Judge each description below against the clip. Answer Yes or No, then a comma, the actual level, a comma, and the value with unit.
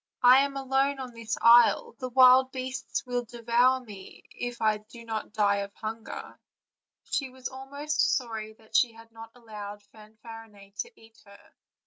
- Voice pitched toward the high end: Yes, high, 235 Hz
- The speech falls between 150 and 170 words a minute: Yes, average, 160 wpm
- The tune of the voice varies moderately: Yes, average, 3.0 semitones